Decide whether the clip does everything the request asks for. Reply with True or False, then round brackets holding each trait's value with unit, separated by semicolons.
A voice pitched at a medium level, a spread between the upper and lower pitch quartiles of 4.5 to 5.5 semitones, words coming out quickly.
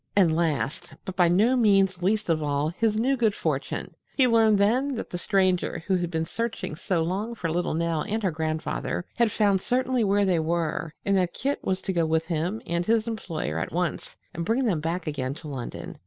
True (180 Hz; 4.9 semitones; 215 wpm)